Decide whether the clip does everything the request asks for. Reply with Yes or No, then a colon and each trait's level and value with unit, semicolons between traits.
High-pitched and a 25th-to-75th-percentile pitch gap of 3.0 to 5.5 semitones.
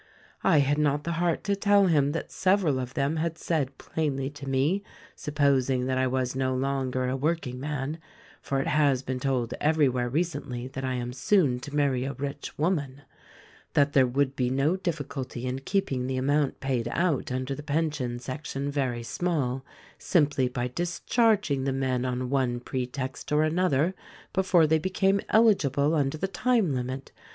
No: medium, 140 Hz; average, 3.5 semitones